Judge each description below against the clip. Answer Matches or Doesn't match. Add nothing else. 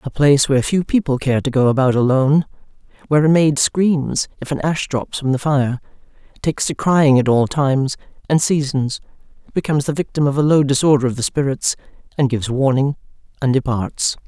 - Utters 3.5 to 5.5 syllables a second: Doesn't match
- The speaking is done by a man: Doesn't match